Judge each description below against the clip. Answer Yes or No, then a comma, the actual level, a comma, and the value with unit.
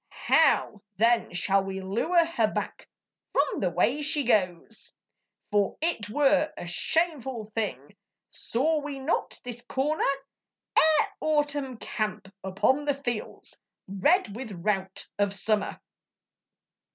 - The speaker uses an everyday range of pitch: No, wide, 6.8 semitones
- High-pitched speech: Yes, high, 235 Hz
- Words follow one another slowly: Yes, slow, 120 wpm